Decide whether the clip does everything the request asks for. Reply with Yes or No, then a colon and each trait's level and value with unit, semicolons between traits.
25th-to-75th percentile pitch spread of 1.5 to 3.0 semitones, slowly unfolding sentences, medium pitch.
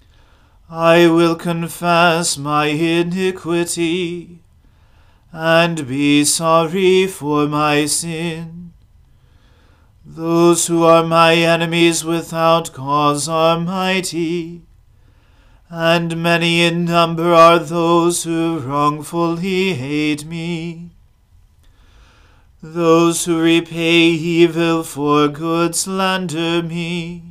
Yes: narrow, 2.5 semitones; slow, 85 wpm; medium, 165 Hz